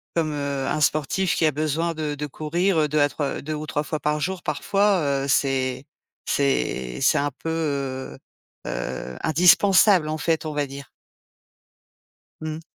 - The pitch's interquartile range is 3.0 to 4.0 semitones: No, narrow, 2.5 semitones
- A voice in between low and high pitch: Yes, medium, 150 Hz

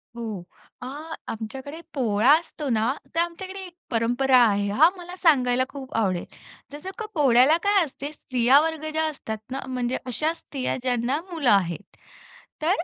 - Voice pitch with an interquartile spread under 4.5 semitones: No, average, 5.1 semitones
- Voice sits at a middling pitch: No, very high, 265 Hz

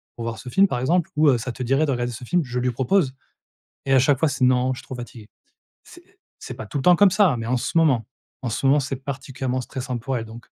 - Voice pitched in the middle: No, low, 130 Hz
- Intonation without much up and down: No, average, 3.1 semitones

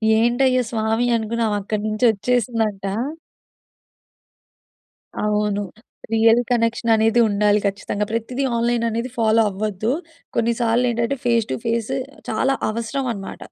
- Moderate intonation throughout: No, narrow, 1.8 semitones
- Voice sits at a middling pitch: No, high, 225 Hz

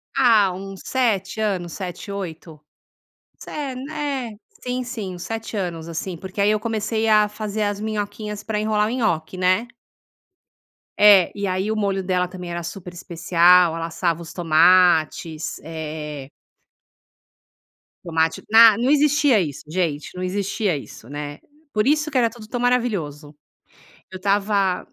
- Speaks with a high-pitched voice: Yes, high, 195 Hz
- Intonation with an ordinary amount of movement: Yes, average, 4.2 semitones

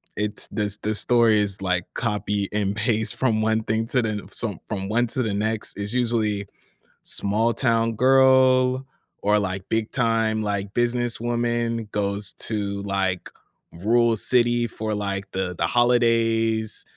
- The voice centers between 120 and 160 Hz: No, low, 110 Hz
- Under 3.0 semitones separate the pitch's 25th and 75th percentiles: Yes, narrow, 2.5 semitones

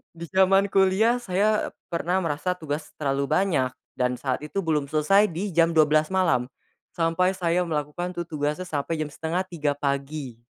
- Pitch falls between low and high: Yes, medium, 165 Hz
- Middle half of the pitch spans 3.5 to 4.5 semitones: Yes, average, 4.0 semitones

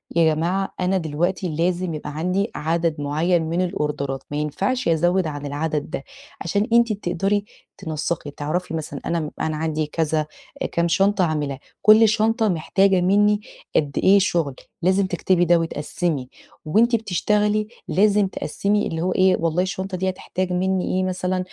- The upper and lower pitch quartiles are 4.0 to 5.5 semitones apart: No, average, 3.6 semitones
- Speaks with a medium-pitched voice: Yes, medium, 175 Hz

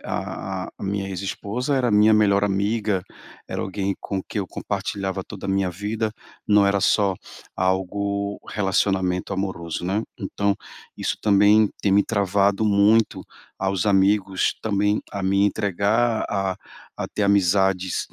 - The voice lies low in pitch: Yes, low, 100 Hz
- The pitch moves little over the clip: Yes, narrow, 1.3 semitones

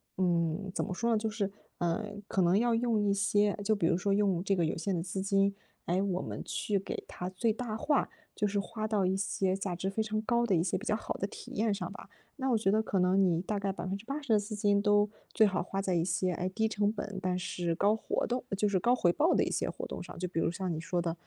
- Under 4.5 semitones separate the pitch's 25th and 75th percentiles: Yes, average, 2.8 semitones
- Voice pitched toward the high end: Yes, high, 200 Hz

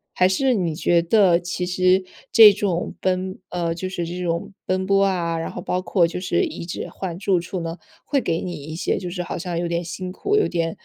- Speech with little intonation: Yes, narrow, 1.9 semitones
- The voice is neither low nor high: Yes, medium, 180 Hz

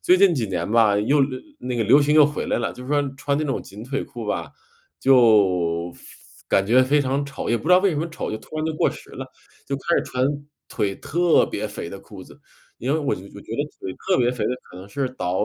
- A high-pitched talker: No, low, 130 Hz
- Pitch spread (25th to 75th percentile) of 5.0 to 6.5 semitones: Yes, wide, 5.4 semitones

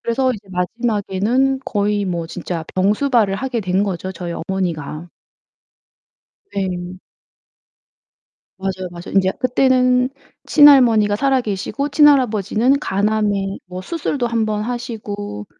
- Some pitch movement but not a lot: Yes, average, 5.0 semitones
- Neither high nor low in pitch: No, high, 205 Hz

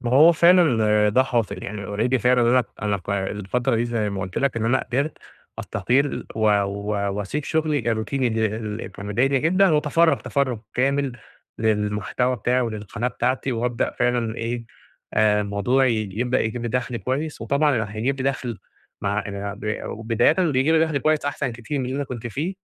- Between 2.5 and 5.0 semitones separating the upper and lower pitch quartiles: Yes, average, 4.1 semitones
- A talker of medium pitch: No, low, 120 Hz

